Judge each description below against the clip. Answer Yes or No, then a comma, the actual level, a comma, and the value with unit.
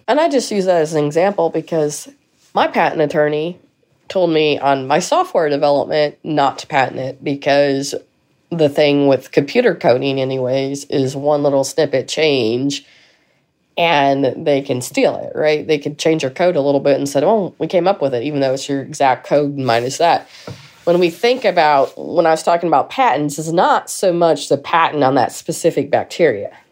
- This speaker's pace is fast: No, average, 190 wpm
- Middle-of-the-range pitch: Yes, medium, 150 Hz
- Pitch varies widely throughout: No, average, 3.3 semitones